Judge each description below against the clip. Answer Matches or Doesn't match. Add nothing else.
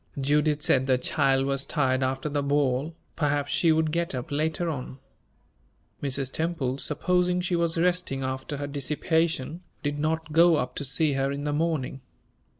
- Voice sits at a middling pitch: Matches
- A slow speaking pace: Doesn't match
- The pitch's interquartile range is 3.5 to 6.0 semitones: Doesn't match